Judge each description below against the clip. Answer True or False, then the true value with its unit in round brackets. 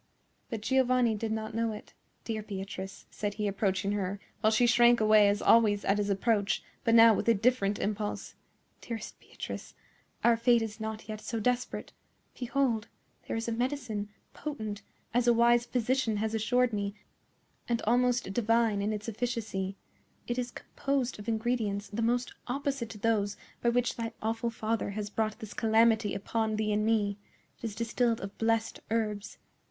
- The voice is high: True (225 Hz)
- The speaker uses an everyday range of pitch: False (2.3 semitones)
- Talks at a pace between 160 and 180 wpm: True (170 wpm)